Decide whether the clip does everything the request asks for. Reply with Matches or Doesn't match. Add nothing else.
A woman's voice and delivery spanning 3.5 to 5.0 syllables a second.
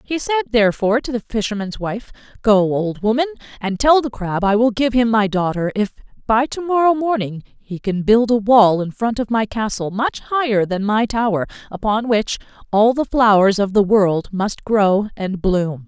Matches